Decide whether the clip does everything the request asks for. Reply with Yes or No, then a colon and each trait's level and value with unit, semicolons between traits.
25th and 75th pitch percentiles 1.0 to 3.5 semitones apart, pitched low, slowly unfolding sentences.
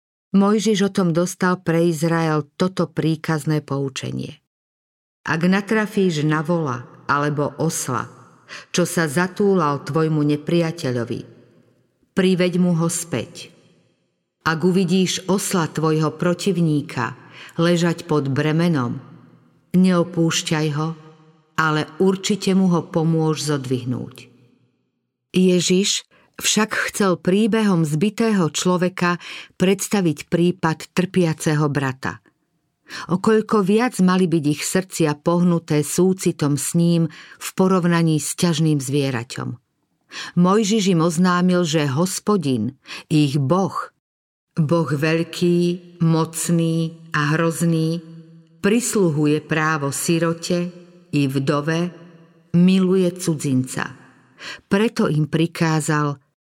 No: average, 3.2 semitones; medium, 165 Hz; slow, 95 wpm